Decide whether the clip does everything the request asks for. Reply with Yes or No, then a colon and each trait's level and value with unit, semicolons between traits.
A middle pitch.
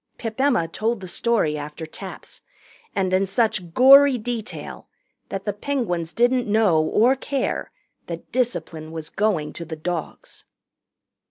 No: high, 200 Hz